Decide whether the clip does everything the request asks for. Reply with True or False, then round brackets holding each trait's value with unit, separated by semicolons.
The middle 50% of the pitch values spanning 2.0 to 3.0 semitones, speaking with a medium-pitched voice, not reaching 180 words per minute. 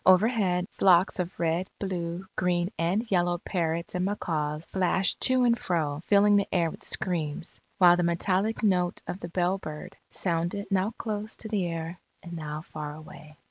True (2.6 semitones; 180 Hz; 165 wpm)